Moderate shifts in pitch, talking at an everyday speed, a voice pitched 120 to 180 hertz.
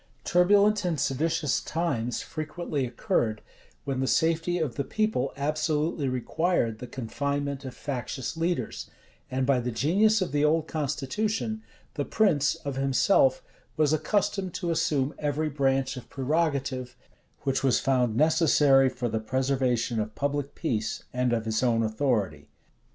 Yes: average, 4.1 semitones; average, 145 wpm; medium, 140 Hz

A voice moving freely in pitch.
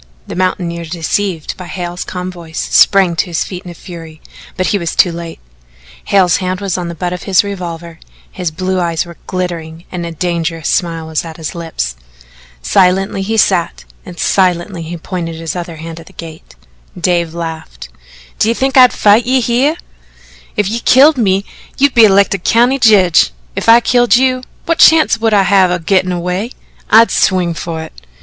No: average, 3.2 semitones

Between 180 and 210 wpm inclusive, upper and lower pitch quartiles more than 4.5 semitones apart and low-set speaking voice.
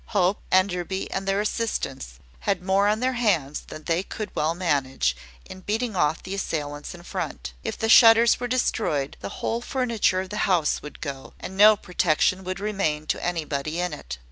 No: average, 185 wpm; wide, 5.4 semitones; medium, 185 Hz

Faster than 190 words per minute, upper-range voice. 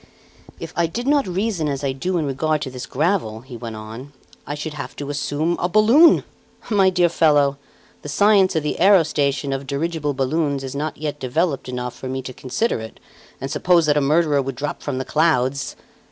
No: average, 200 wpm; medium, 145 Hz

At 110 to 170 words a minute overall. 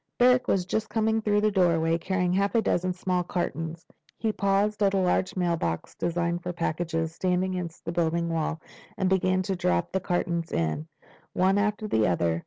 No: average, 185 wpm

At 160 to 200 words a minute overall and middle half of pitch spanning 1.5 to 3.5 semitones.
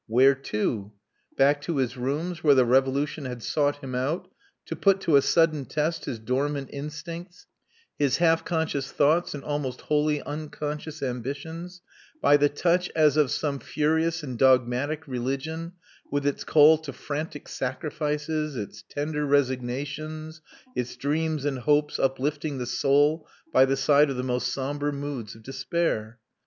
No: average, 150 wpm; average, 2.7 semitones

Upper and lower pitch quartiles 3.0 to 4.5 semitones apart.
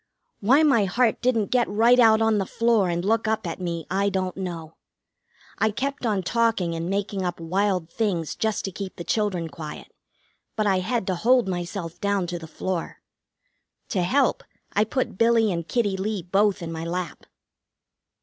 Yes: average, 4.1 semitones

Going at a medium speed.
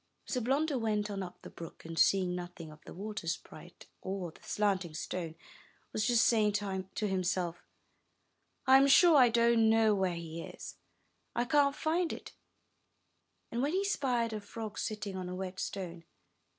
Yes: average, 170 wpm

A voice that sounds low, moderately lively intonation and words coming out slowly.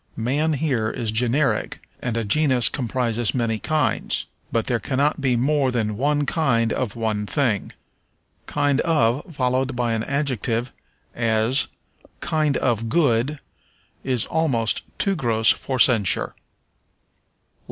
Yes: low, 125 Hz; average, 4.0 semitones; slow, 125 wpm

